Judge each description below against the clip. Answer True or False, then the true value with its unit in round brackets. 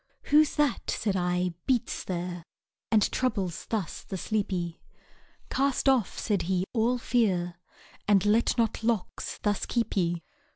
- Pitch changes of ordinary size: True (4.7 semitones)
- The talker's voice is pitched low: False (205 Hz)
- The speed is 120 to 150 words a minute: True (135 wpm)